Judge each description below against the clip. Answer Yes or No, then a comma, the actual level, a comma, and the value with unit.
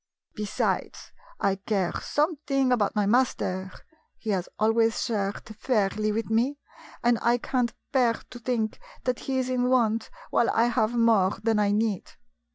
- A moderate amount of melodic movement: Yes, average, 3.0 semitones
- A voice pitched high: Yes, high, 225 Hz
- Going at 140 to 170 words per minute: Yes, average, 165 wpm